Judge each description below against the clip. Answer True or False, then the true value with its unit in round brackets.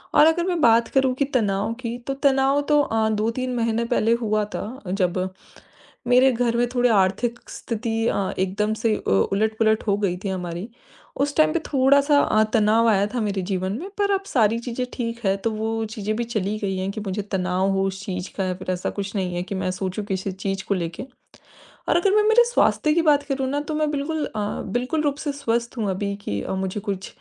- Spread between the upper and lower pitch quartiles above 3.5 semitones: True (5.1 semitones)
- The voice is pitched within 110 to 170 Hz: False (220 Hz)